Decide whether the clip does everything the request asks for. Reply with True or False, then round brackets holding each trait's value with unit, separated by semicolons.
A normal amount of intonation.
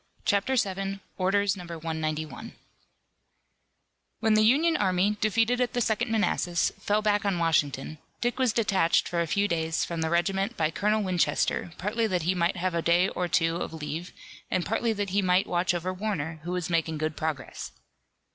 True (3.9 semitones)